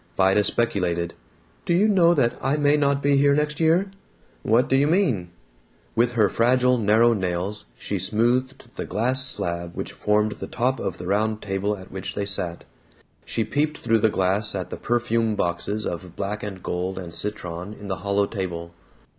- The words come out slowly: No, average, 180 wpm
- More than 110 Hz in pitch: No, low, 105 Hz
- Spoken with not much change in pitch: No, average, 5.2 semitones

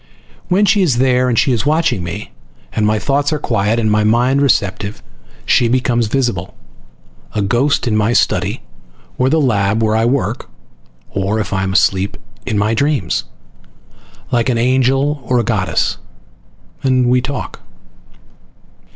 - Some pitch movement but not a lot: Yes, average, 4.0 semitones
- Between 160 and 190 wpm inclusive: No, average, 150 wpm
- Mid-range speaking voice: No, low, 120 Hz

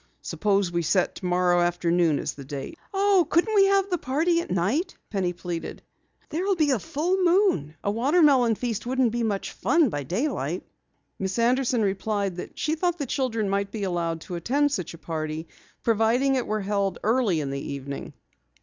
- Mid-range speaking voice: No, high, 220 Hz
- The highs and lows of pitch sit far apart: Yes, wide, 8.6 semitones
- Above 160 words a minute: Yes, average, 185 wpm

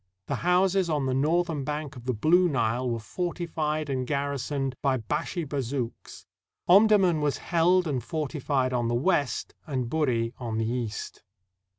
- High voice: No, medium, 140 Hz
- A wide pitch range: No, average, 4.7 semitones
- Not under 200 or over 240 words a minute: No, average, 155 wpm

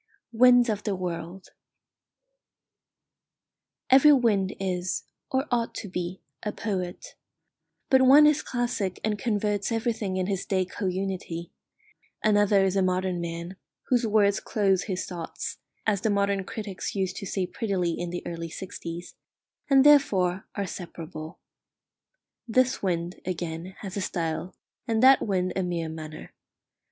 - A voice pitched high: Yes, high, 195 Hz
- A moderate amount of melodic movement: Yes, average, 3.4 semitones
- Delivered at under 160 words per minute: Yes, average, 140 wpm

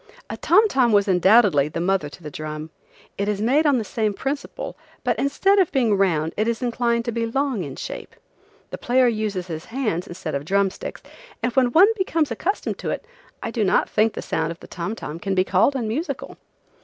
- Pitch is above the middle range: Yes, high, 215 Hz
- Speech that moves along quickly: Yes, fast, 210 wpm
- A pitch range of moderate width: No, wide, 6.1 semitones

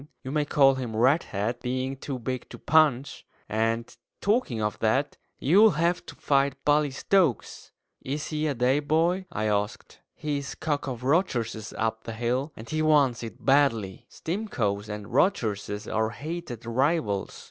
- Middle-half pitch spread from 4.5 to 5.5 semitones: Yes, average, 5.0 semitones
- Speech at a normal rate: Yes, average, 155 wpm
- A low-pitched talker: Yes, low, 130 Hz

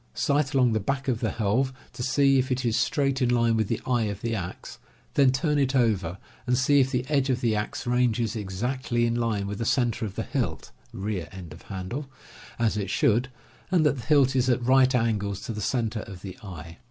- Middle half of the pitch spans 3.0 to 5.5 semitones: Yes, average, 3.9 semitones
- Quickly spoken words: Yes, fast, 230 wpm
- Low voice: Yes, low, 120 Hz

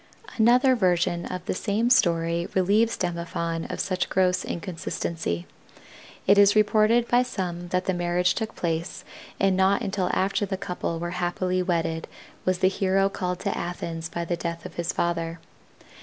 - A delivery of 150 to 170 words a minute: Yes, average, 160 wpm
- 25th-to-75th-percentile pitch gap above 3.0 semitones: No, narrow, 2.5 semitones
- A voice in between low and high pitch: Yes, medium, 180 Hz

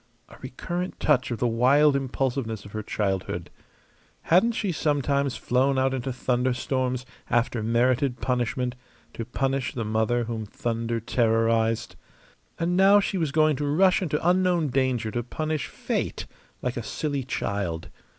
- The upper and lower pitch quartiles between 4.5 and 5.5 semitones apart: No, average, 4.0 semitones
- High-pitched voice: No, low, 130 Hz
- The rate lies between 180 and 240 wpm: No, average, 145 wpm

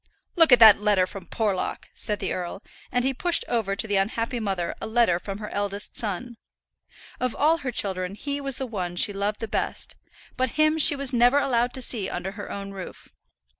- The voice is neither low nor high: No, high, 220 Hz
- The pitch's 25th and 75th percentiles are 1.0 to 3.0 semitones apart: No, average, 4.3 semitones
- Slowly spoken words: No, fast, 205 wpm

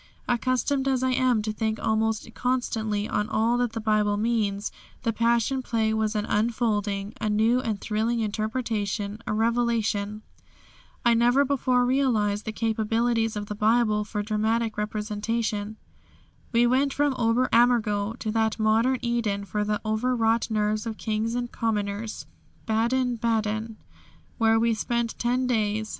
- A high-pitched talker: Yes, high, 225 Hz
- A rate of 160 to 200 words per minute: No, average, 145 wpm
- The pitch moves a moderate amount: No, narrow, 1.9 semitones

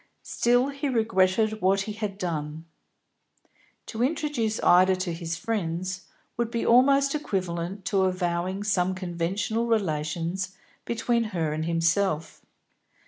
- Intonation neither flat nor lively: Yes, average, 4.8 semitones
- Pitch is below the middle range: No, high, 190 Hz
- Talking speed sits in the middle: No, slow, 120 wpm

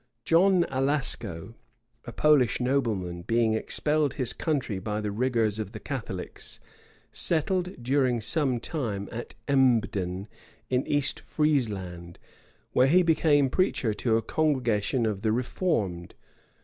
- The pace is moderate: No, slow, 125 wpm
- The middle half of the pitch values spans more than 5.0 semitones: Yes, wide, 5.6 semitones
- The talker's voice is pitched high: No, low, 125 Hz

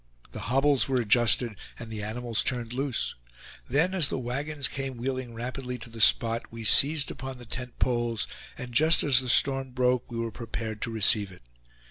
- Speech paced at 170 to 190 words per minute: Yes, average, 185 wpm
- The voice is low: Yes, low, 125 Hz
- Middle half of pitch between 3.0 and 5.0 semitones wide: No, narrow, 2.5 semitones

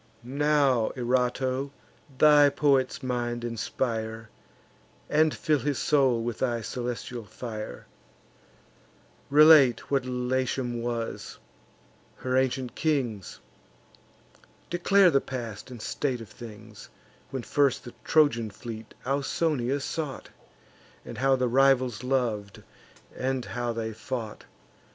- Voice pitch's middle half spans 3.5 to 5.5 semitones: No, average, 2.8 semitones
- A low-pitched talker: Yes, low, 125 Hz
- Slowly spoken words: Yes, slow, 110 wpm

